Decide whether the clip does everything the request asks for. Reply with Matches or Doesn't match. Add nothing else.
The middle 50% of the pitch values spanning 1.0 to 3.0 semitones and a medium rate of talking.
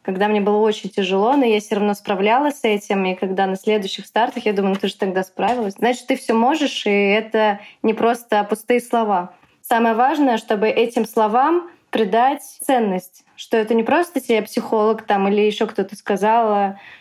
Doesn't match